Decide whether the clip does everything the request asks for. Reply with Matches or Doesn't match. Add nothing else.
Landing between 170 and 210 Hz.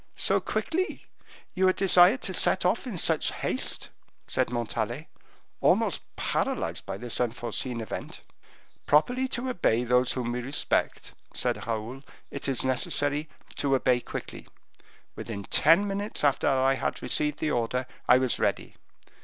Doesn't match